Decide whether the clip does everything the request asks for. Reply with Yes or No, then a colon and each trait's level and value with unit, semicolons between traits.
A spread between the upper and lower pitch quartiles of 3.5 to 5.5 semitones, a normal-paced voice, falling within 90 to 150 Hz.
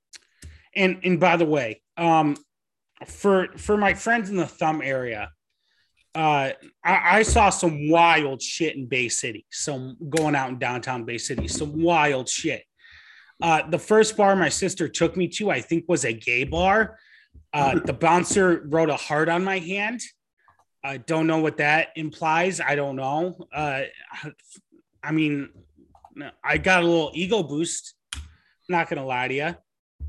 No: average, 4.1 semitones; average, 160 wpm; medium, 160 Hz